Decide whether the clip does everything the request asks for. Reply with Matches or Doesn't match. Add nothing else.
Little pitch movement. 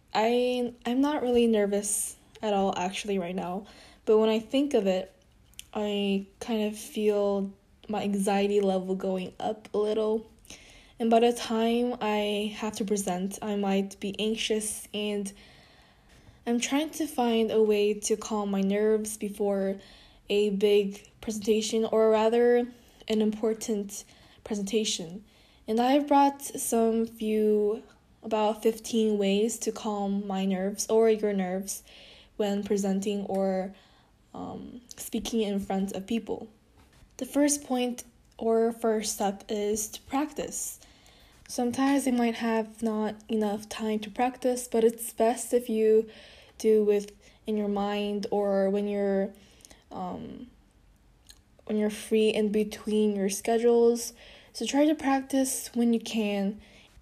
Matches